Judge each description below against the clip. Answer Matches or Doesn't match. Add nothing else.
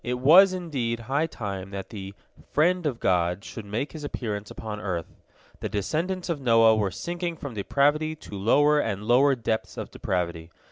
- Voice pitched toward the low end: Matches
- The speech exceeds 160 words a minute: Matches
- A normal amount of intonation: Doesn't match